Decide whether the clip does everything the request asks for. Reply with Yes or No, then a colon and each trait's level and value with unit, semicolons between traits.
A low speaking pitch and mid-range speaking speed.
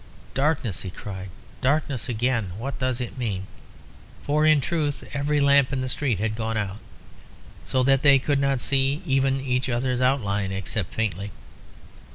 Yes: low, 130 Hz; average, 160 wpm